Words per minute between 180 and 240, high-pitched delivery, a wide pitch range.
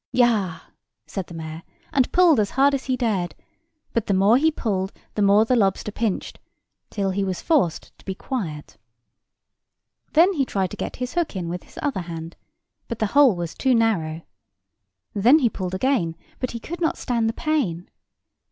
Yes: average, 185 wpm; high, 215 Hz; wide, 5.9 semitones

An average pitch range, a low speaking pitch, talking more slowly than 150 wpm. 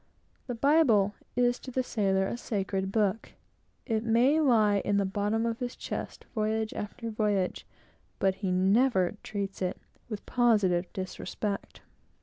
No: average, 3.4 semitones; high, 215 Hz; average, 140 wpm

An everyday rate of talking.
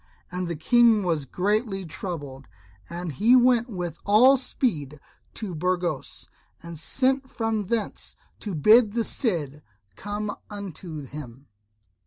No: slow, 125 wpm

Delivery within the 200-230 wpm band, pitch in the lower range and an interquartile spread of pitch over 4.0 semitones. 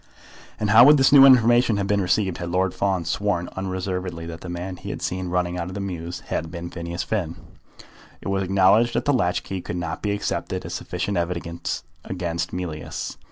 No: fast, 205 wpm; very low, 90 Hz; average, 2.8 semitones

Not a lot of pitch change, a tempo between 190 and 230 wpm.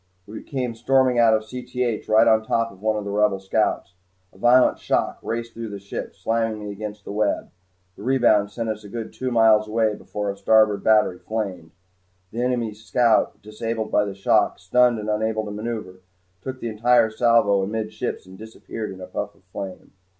Yes: narrow, 2.0 semitones; average, 195 wpm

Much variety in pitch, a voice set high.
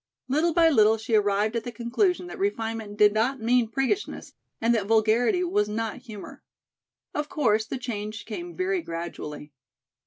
No: average, 5.0 semitones; high, 225 Hz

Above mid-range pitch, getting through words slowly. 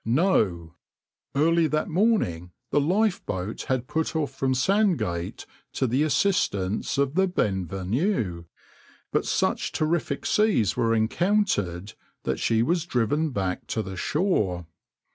No: low, 130 Hz; slow, 125 wpm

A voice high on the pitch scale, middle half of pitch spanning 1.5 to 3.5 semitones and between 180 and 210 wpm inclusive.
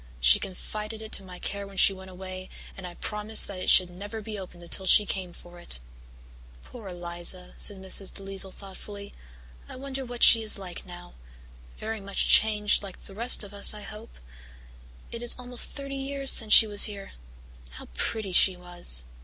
Yes: high, 200 Hz; average, 2.9 semitones; average, 190 wpm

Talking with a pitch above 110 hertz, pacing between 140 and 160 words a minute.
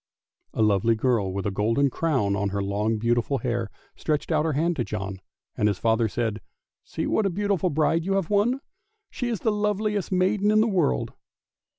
No: medium, 140 Hz; average, 200 wpm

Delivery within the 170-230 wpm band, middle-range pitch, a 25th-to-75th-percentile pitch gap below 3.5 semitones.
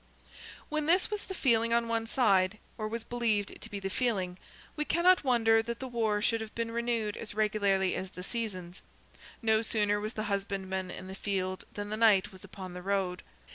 No: average, 200 wpm; high, 215 Hz; average, 3.1 semitones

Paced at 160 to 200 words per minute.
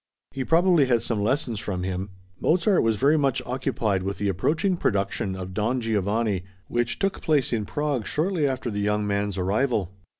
Yes: average, 175 wpm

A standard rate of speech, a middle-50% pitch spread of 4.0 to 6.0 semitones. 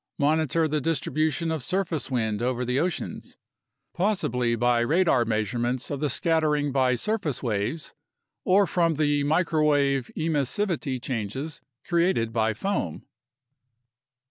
No: slow, 115 wpm; average, 5.0 semitones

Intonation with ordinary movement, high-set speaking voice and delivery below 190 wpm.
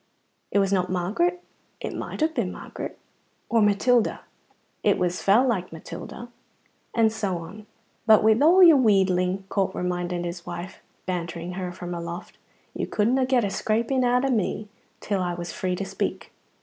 Yes: average, 4.7 semitones; high, 195 Hz; average, 165 wpm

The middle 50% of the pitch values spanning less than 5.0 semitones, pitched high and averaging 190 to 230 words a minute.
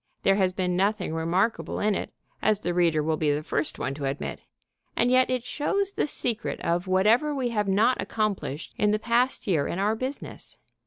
No: wide, 5.4 semitones; high, 205 Hz; average, 200 wpm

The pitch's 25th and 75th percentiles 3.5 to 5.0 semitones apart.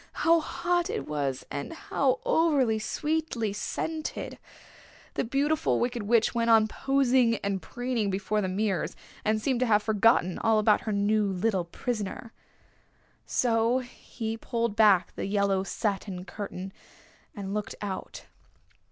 Yes: average, 4.0 semitones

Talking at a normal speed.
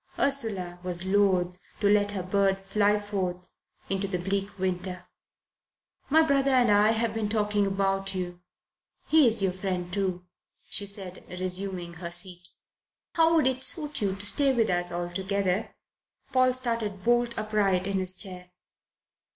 Yes: average, 150 wpm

